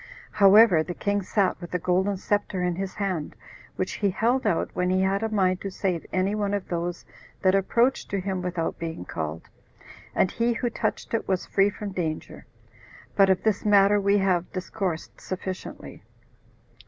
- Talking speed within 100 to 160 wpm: No, average, 180 wpm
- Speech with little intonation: Yes, narrow, 2.1 semitones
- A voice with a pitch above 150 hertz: Yes, high, 190 Hz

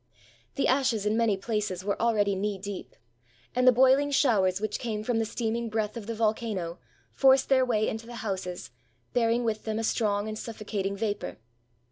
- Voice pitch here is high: Yes, high, 220 Hz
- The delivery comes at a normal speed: Yes, average, 180 wpm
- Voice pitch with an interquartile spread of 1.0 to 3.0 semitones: Yes, narrow, 2.5 semitones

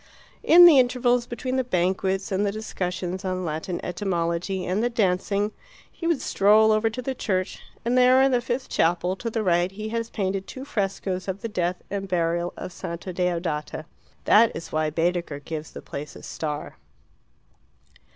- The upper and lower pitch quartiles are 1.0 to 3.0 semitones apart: No, average, 4.7 semitones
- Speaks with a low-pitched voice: No, high, 190 Hz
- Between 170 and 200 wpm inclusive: Yes, average, 175 wpm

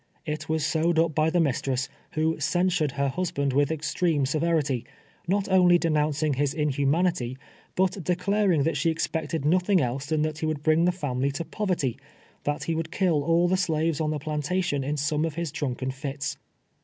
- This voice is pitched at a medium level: Yes, medium, 155 Hz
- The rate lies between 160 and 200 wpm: Yes, average, 185 wpm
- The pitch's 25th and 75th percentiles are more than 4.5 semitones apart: No, average, 3.0 semitones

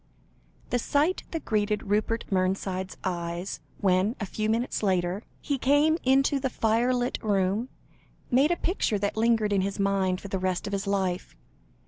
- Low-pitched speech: No, high, 205 Hz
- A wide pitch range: No, average, 4.5 semitones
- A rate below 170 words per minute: Yes, average, 160 wpm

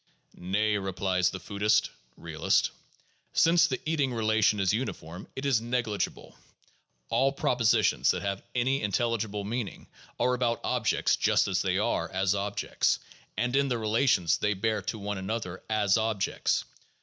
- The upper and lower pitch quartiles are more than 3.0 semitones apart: Yes, average, 3.6 semitones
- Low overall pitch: Yes, low, 110 Hz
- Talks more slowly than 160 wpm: Yes, average, 150 wpm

